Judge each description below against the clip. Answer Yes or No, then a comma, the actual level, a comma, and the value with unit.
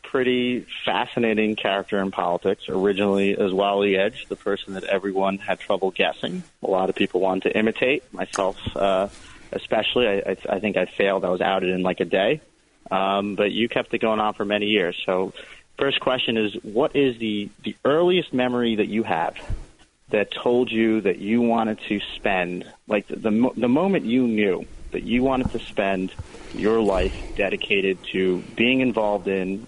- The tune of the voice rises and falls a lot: No, average, 3.3 semitones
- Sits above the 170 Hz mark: No, low, 105 Hz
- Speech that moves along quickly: No, average, 180 wpm